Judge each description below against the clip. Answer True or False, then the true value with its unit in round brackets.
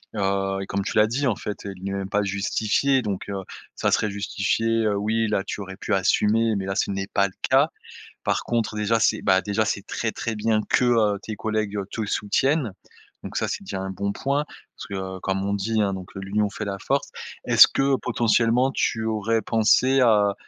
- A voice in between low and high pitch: False (105 Hz)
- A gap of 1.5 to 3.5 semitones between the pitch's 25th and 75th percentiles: True (2.5 semitones)